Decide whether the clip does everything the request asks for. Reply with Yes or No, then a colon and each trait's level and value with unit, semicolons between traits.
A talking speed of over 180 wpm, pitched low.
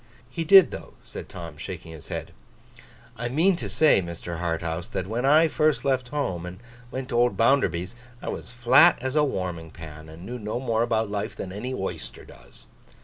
Yes: average, 200 wpm; low, 115 Hz